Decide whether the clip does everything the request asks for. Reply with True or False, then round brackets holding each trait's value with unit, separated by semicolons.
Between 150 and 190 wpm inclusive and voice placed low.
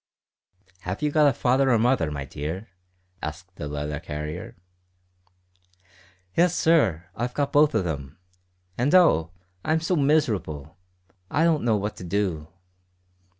False (140 wpm; 105 Hz)